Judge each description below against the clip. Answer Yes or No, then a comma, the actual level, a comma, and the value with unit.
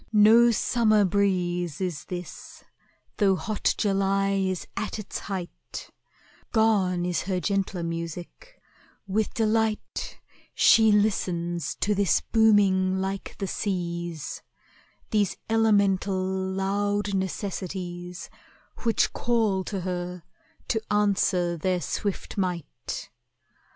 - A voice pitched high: Yes, high, 195 Hz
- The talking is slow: Yes, slow, 100 wpm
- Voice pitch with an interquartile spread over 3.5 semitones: No, narrow, 2.6 semitones